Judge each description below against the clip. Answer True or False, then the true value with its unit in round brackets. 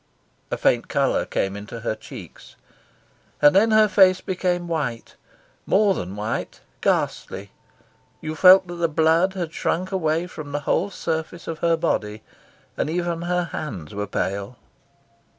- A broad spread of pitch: True (7.4 semitones)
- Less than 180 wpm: True (150 wpm)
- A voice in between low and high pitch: True (165 Hz)